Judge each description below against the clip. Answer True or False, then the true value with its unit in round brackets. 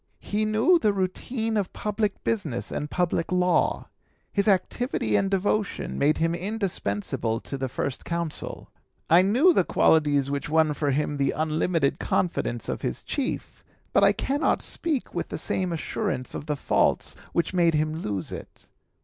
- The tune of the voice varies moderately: False (5.8 semitones)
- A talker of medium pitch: True (170 Hz)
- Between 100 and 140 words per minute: False (160 wpm)